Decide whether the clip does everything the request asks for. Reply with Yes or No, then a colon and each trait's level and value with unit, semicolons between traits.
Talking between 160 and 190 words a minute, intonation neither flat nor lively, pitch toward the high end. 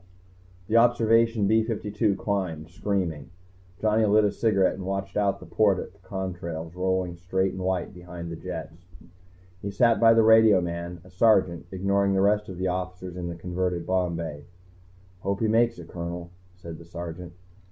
No: average, 175 wpm; average, 3.0 semitones; very low, 95 Hz